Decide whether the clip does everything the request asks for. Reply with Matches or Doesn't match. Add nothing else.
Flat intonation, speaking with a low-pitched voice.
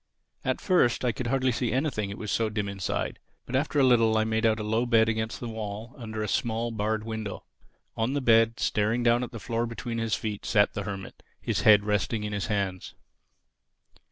Matches